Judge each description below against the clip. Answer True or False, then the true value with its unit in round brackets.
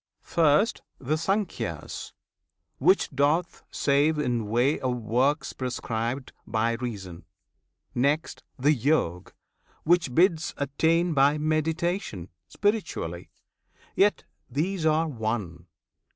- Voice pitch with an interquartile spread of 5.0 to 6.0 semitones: True (5.4 semitones)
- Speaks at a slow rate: True (95 wpm)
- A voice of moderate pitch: True (145 Hz)